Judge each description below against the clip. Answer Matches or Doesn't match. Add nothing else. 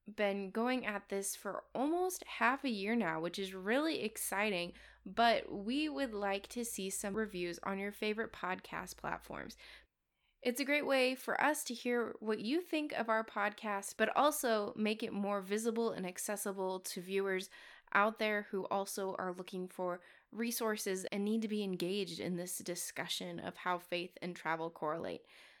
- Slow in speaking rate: Doesn't match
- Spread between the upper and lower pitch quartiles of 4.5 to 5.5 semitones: Doesn't match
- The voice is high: Matches